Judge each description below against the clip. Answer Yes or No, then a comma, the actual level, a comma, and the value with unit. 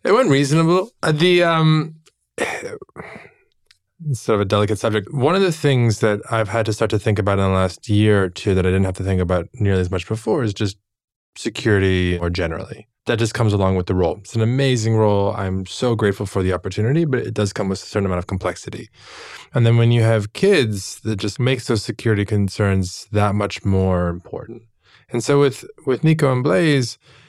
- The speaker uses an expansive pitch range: No, average, 4.6 semitones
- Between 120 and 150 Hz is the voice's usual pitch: No, low, 110 Hz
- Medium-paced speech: No, fast, 210 wpm